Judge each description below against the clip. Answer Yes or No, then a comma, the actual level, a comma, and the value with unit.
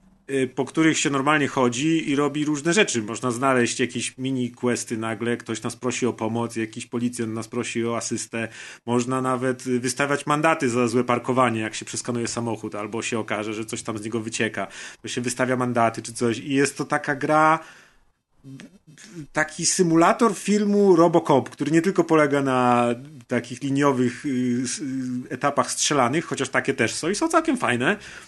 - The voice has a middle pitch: No, low, 130 Hz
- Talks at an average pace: No, fast, 165 wpm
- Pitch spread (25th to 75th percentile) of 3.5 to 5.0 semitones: Yes, average, 3.9 semitones